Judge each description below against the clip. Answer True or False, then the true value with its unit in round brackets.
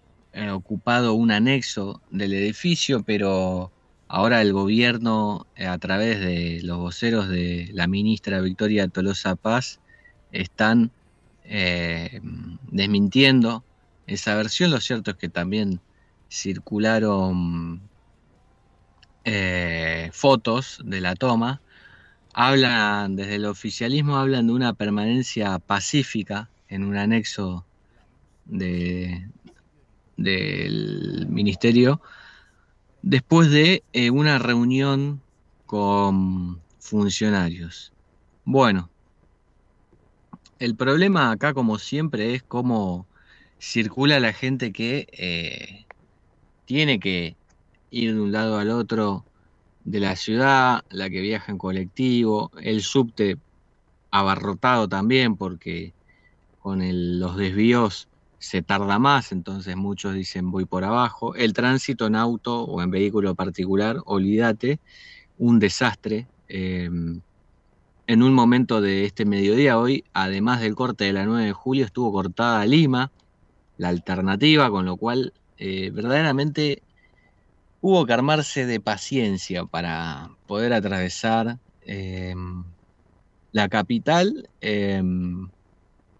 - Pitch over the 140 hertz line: False (105 Hz)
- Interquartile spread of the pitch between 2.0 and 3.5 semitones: False (4.4 semitones)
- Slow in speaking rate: True (105 wpm)